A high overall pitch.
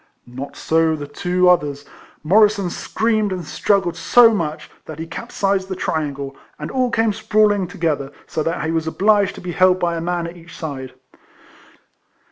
No: medium, 175 Hz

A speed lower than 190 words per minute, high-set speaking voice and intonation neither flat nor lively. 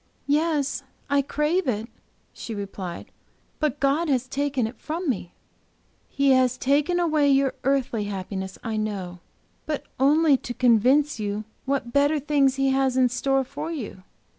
Yes: average, 150 wpm; very high, 270 Hz; average, 4.0 semitones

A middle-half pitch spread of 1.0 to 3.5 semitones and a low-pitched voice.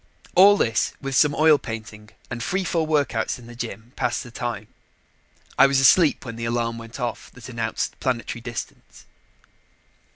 Yes: average, 3.2 semitones; low, 120 Hz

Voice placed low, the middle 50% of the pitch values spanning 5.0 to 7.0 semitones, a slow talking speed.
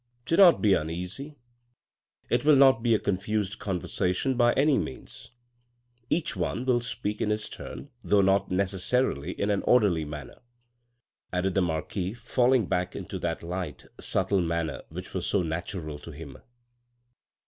No: low, 100 Hz; average, 5.3 semitones; average, 155 wpm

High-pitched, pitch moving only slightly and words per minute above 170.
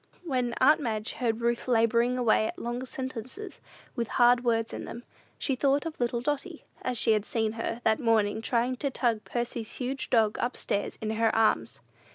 Yes: high, 240 Hz; narrow, 2.3 semitones; average, 190 wpm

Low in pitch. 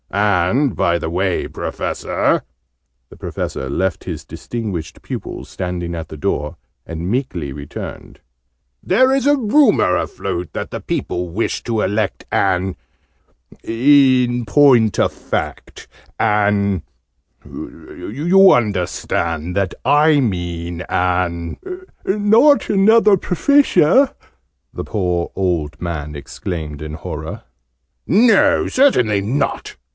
Yes: low, 100 Hz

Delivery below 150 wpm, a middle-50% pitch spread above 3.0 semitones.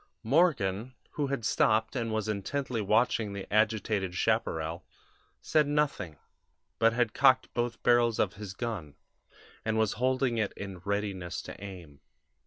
Yes: average, 140 wpm; average, 3.9 semitones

